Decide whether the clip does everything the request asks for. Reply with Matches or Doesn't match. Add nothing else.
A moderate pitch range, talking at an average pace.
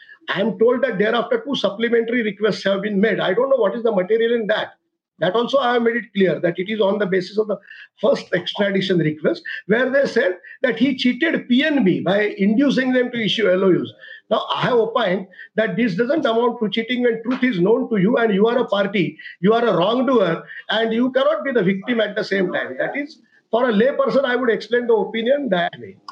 Doesn't match